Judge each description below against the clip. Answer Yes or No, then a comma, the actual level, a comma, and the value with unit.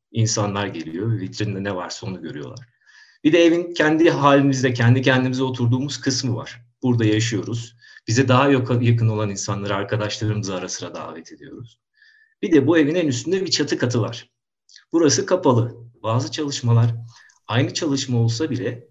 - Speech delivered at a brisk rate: Yes, fast, 150 wpm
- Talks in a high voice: No, low, 120 Hz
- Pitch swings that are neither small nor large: Yes, average, 3.8 semitones